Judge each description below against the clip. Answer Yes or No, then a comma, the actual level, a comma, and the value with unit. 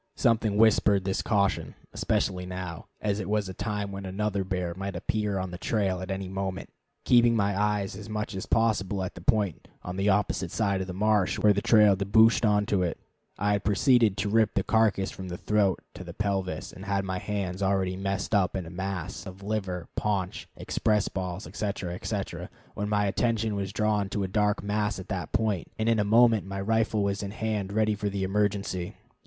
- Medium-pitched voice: No, low, 100 Hz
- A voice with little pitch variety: Yes, narrow, 1.9 semitones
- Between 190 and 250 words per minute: Yes, fast, 205 wpm